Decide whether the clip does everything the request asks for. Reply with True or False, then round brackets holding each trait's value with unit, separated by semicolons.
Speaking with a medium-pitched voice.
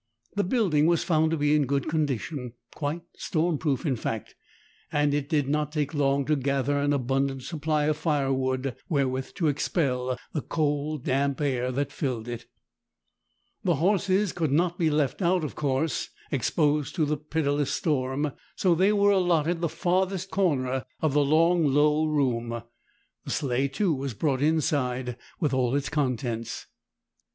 True (145 Hz)